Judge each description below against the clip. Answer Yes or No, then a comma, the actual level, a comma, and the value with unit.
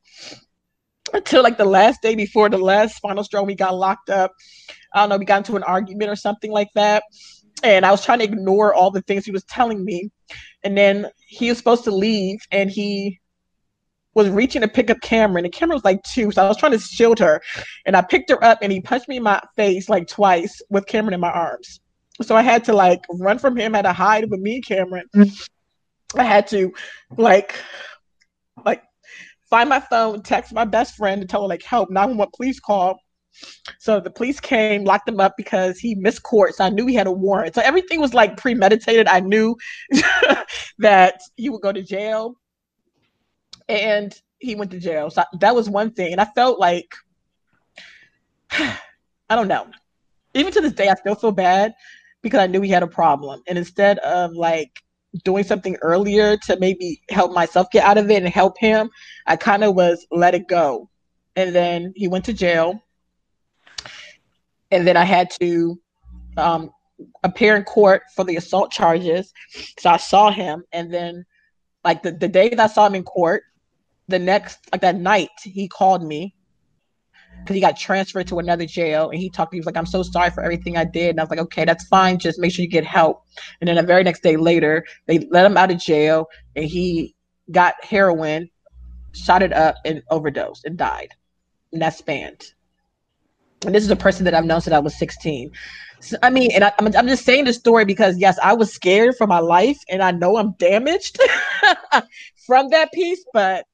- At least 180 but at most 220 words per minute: Yes, fast, 205 wpm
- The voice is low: No, high, 195 Hz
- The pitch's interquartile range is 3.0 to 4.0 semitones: Yes, average, 3.7 semitones